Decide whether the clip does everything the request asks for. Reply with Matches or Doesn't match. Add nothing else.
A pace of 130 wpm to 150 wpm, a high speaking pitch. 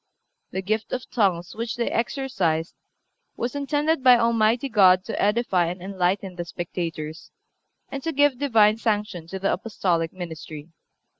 Matches